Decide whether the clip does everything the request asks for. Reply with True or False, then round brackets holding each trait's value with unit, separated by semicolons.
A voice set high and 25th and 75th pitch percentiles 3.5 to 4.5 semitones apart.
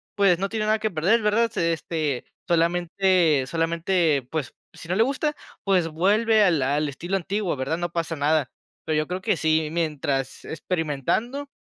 False (170 Hz; 4.2 semitones)